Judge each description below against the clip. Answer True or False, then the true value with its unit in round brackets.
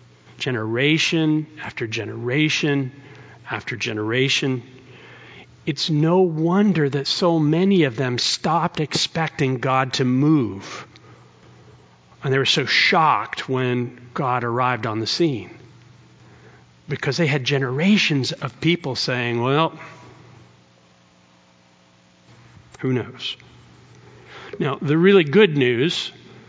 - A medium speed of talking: False (100 wpm)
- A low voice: True (130 Hz)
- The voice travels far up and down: True (5.7 semitones)